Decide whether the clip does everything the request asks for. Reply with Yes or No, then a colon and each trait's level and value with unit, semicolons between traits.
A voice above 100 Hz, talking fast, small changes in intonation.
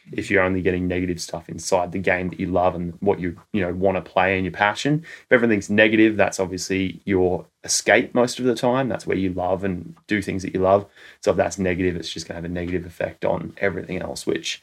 No: very low, 95 Hz; fast, 245 wpm; narrow, 2.0 semitones